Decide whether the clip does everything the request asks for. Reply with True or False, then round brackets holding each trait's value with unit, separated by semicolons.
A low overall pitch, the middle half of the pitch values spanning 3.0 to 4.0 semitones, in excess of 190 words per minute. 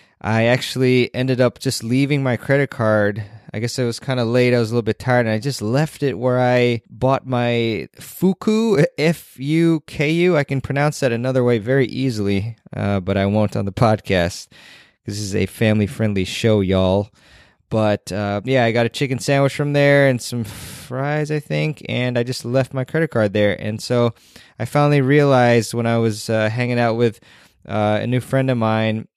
True (120 Hz; 3.7 semitones; 205 wpm)